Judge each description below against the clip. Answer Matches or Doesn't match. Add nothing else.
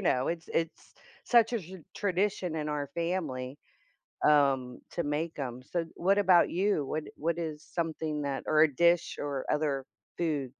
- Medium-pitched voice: Matches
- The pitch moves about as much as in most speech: Matches